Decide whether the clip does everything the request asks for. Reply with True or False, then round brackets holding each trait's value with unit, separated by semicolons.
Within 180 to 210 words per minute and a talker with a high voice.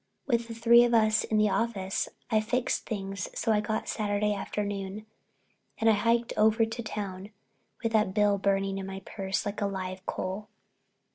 False (170 wpm; 210 Hz)